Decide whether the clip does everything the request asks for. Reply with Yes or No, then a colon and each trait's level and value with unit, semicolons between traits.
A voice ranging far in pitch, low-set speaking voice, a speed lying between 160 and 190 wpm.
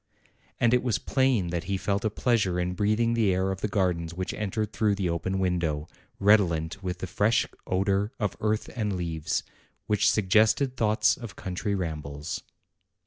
No: average, 3.2 semitones; low, 100 Hz; average, 170 wpm